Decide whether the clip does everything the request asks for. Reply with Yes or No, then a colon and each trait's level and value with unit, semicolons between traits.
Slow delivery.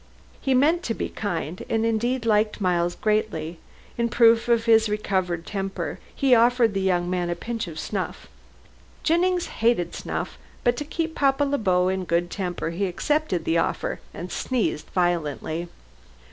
No: average, 165 wpm